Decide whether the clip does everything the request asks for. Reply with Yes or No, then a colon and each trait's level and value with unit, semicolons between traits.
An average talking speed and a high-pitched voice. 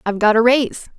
No: fast, 245 wpm; high, 230 Hz